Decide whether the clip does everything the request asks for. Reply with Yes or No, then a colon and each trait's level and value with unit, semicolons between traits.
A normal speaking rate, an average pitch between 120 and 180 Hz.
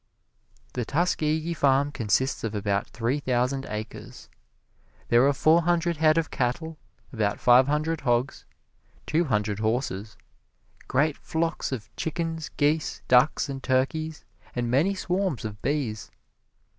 No: slow, 130 wpm; medium, 140 Hz